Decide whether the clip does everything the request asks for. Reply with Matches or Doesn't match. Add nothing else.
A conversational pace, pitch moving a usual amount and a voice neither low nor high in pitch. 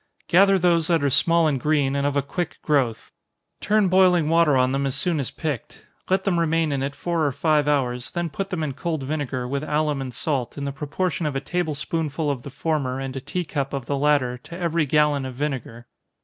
Doesn't match